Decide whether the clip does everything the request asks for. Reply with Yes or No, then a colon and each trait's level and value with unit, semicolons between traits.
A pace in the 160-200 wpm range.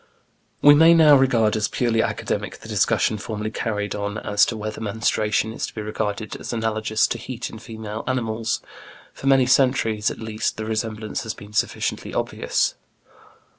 Yes: average, 170 wpm